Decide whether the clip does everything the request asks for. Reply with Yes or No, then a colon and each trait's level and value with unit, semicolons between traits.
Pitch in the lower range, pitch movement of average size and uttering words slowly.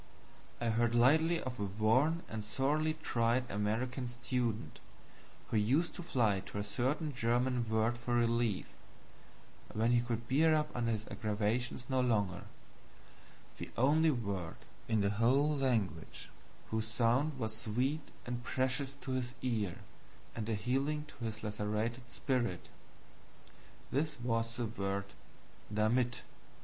Yes: low, 120 Hz; average, 3.0 semitones; slow, 125 wpm